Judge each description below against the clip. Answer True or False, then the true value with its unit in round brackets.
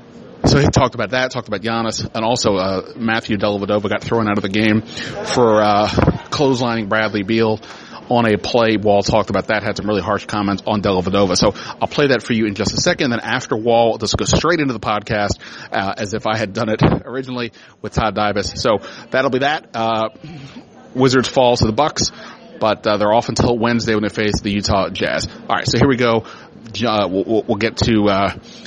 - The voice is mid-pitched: False (110 Hz)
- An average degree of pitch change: False (2.1 semitones)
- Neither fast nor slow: False (210 wpm)